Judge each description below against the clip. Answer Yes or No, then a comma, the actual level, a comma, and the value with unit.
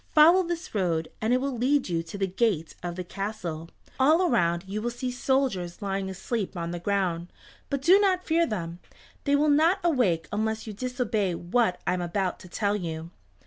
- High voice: Yes, high, 210 Hz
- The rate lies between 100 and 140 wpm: No, average, 195 wpm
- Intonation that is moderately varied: No, wide, 7.0 semitones